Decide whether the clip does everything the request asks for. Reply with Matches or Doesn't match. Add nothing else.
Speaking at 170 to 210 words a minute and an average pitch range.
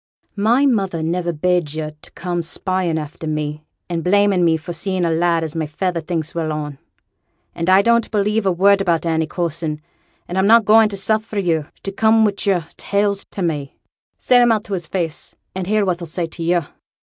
Matches